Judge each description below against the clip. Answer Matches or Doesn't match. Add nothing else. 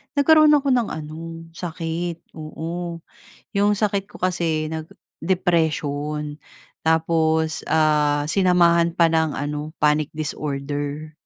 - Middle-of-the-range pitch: Matches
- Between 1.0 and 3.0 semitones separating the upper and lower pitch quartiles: Matches